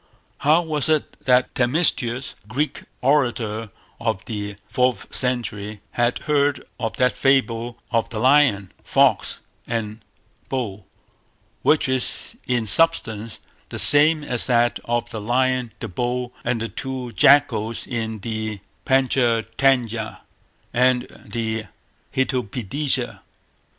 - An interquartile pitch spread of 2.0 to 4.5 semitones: Yes, average, 2.9 semitones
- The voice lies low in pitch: Yes, low, 120 Hz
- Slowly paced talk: Yes, slow, 120 wpm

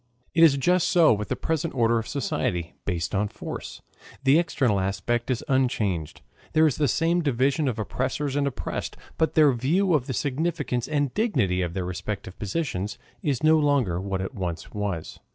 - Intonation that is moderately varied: No, wide, 7.2 semitones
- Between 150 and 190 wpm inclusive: Yes, average, 180 wpm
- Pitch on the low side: Yes, low, 130 Hz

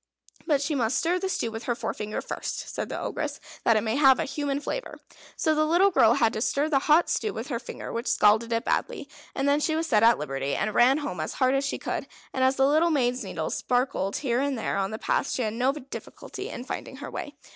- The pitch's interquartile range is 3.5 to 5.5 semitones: Yes, average, 4.3 semitones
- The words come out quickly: Yes, fast, 250 wpm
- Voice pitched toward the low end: No, very high, 260 Hz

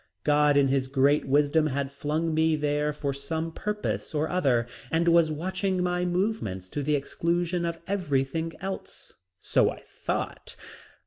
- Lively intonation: No, average, 3.5 semitones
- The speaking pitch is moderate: Yes, medium, 155 Hz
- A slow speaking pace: No, average, 150 wpm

